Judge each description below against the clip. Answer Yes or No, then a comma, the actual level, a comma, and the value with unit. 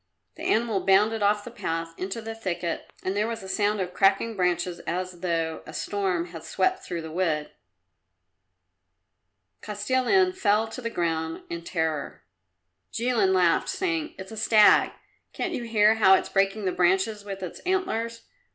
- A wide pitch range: No, average, 4.2 semitones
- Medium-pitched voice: No, high, 195 Hz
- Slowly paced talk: No, average, 160 wpm